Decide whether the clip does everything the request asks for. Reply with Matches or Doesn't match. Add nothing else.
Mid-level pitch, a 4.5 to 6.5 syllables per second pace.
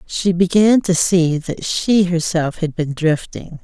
Doesn't match